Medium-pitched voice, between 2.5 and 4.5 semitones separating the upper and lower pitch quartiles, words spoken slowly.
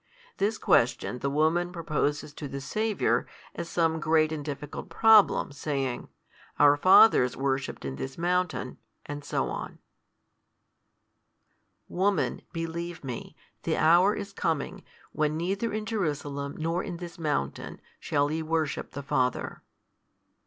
Yes: medium, 160 Hz; average, 3.7 semitones; slow, 125 wpm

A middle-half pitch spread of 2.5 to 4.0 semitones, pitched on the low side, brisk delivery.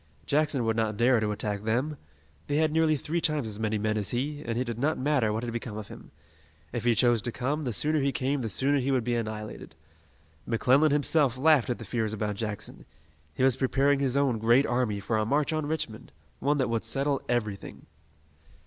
No: average, 4.4 semitones; low, 125 Hz; fast, 215 wpm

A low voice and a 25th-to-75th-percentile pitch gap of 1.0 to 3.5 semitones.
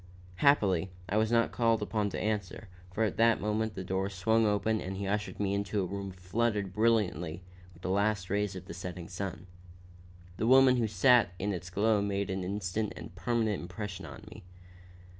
Yes: low, 100 Hz; average, 2.8 semitones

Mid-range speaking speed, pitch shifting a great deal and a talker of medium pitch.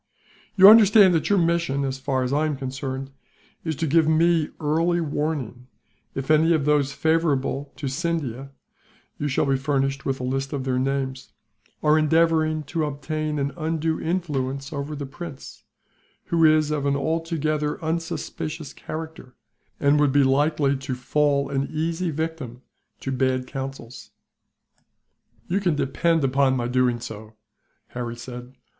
No: average, 150 wpm; average, 3.1 semitones; medium, 145 Hz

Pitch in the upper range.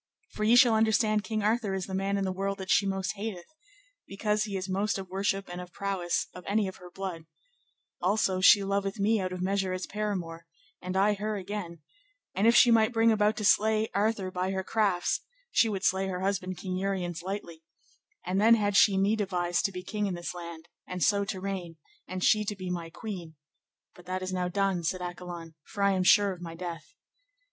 Yes: high, 195 Hz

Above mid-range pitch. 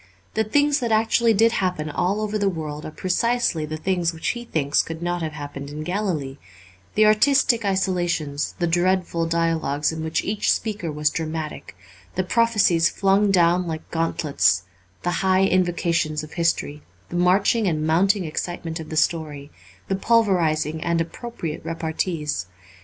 No: medium, 170 Hz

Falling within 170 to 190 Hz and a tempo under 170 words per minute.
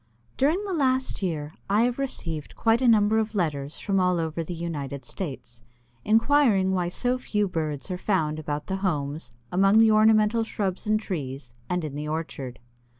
No: medium, 185 Hz; average, 175 wpm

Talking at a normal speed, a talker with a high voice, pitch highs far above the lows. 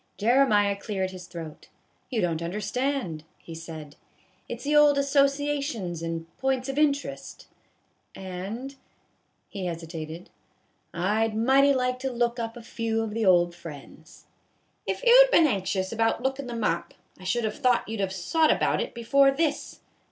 Yes: average, 180 wpm; high, 225 Hz; wide, 7.1 semitones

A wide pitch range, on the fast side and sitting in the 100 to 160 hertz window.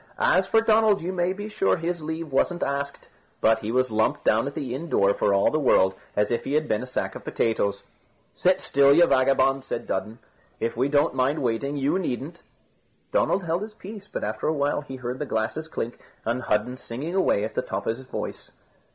Yes: wide, 6.3 semitones; fast, 220 wpm; medium, 140 Hz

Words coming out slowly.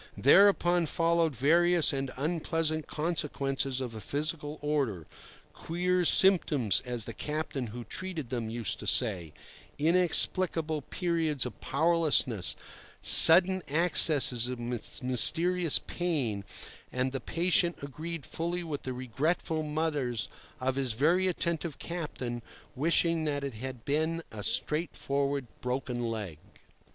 Yes: slow, 115 wpm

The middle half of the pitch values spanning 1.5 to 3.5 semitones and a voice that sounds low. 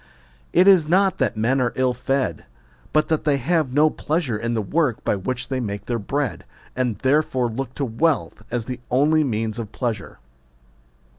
No: average, 4.4 semitones; low, 130 Hz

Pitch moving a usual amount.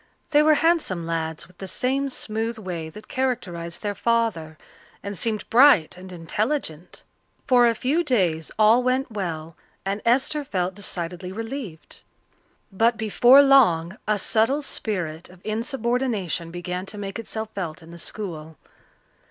No: wide, 5.9 semitones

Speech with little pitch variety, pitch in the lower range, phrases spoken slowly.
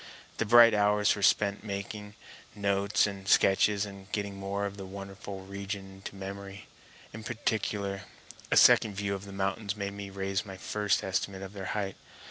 No: narrow, 1.0 semitones; low, 100 Hz; average, 175 wpm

